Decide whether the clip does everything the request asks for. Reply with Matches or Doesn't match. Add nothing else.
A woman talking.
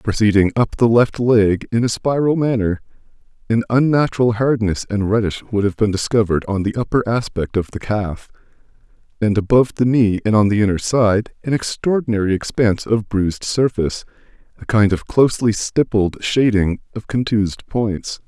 Doesn't match